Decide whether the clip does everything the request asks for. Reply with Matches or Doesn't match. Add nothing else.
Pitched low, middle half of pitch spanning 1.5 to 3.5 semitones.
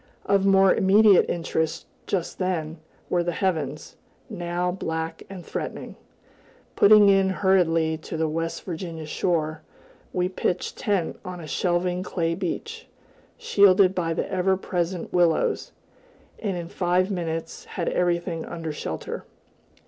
Doesn't match